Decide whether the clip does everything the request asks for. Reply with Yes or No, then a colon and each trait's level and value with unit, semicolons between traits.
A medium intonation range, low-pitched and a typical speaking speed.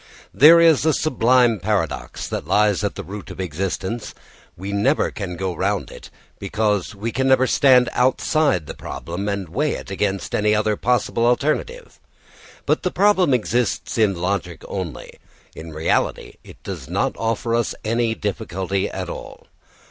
Yes: average, 4.5 semitones; low, 105 Hz; average, 155 wpm